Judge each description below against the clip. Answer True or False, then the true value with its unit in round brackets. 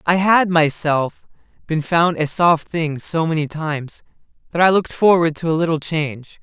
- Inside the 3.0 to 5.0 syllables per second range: True (4.8 syllables/s)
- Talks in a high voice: False (160 Hz)